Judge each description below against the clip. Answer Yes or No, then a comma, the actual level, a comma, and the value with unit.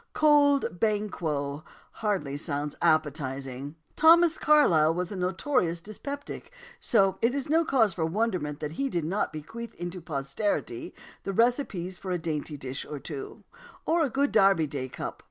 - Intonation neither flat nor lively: No, wide, 7.6 semitones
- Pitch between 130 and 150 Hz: No, medium, 180 Hz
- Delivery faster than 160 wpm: No, average, 155 wpm